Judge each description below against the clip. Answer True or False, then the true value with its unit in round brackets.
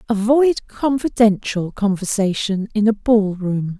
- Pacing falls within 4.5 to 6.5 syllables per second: False (3.9 syllables/s)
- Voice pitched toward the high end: True (215 Hz)